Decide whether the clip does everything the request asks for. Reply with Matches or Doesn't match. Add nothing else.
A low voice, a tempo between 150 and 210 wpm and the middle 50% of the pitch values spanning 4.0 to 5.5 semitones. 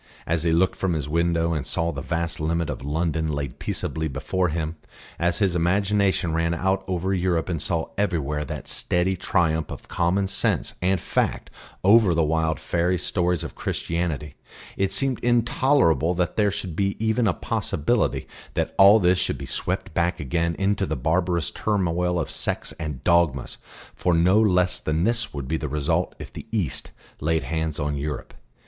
Doesn't match